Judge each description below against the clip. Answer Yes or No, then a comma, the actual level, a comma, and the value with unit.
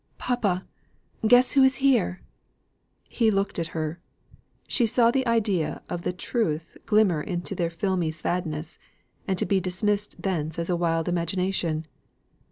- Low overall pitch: No, medium, 180 Hz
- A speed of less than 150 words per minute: Yes, average, 140 wpm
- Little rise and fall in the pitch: No, average, 4.5 semitones